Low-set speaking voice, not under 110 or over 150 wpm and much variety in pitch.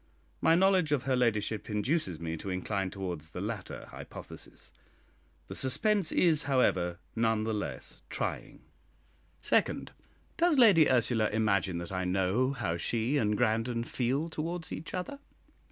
Yes: low, 115 Hz; average, 140 wpm; wide, 7.5 semitones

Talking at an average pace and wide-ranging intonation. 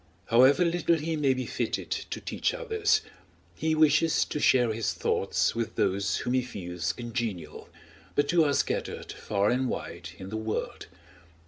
Yes: average, 160 wpm; wide, 6.5 semitones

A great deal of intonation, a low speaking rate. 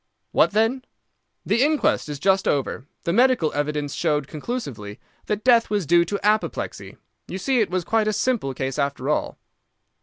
No: wide, 7.4 semitones; average, 170 wpm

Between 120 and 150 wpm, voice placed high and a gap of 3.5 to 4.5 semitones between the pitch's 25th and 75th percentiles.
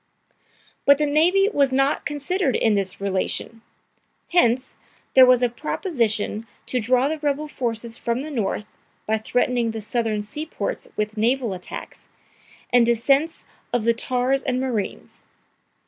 Yes: average, 145 wpm; very high, 250 Hz; average, 4.1 semitones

